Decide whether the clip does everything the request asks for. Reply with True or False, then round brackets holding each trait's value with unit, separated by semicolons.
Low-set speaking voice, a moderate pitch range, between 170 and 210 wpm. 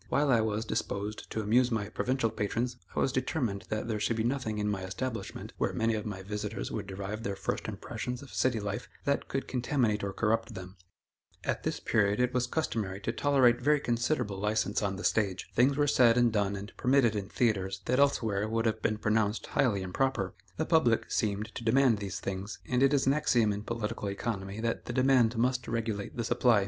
True (115 Hz; 3.4 semitones; 205 wpm)